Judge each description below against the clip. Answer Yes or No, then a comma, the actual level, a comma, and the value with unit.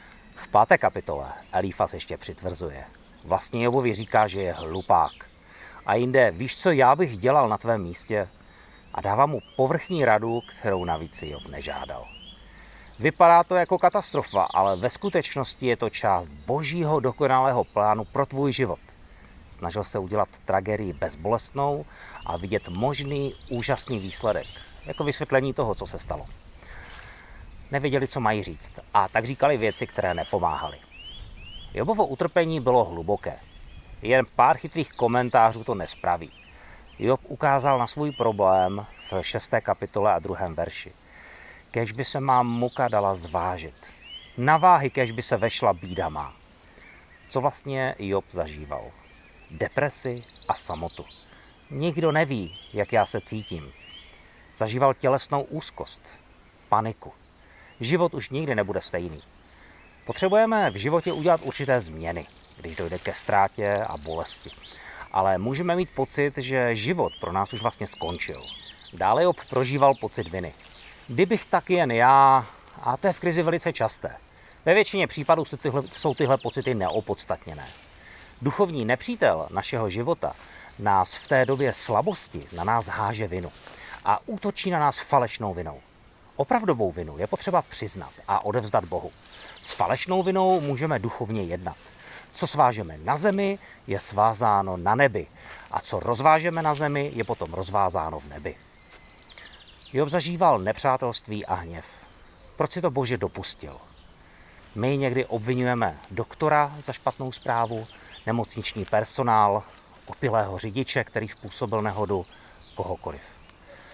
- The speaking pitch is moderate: No, low, 115 Hz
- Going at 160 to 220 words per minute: No, average, 135 wpm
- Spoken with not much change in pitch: No, wide, 7.3 semitones